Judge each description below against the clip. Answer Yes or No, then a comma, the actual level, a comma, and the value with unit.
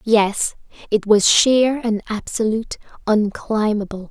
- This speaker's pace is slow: Yes, slow, 100 wpm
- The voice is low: No, high, 215 Hz